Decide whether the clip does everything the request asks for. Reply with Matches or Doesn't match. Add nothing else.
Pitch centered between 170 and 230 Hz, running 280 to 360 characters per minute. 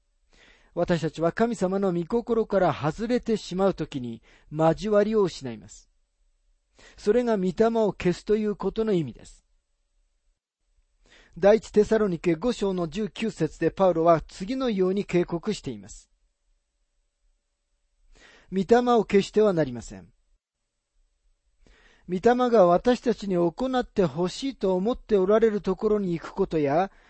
Doesn't match